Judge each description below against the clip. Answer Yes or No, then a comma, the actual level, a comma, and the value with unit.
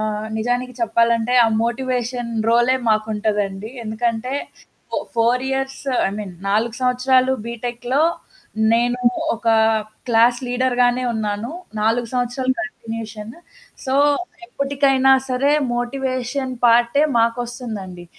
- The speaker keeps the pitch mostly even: Yes, narrow, 2.3 semitones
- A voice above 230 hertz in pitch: Yes, high, 240 Hz